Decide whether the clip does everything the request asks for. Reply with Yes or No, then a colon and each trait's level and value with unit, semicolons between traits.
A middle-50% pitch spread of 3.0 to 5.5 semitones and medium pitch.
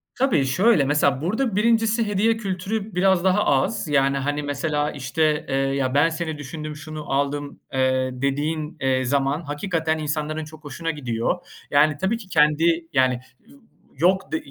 Yes: average, 4.4 semitones; medium, 155 Hz